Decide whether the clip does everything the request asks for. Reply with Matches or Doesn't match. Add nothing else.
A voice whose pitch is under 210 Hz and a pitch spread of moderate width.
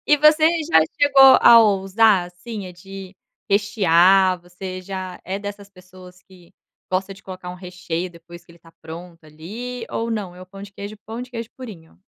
Matches